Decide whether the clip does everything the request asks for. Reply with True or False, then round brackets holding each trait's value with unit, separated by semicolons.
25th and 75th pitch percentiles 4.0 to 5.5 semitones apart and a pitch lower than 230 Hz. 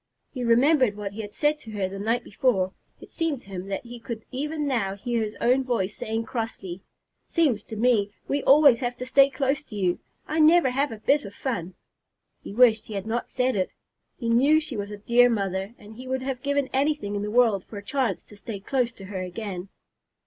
False (4.6 semitones; 235 Hz)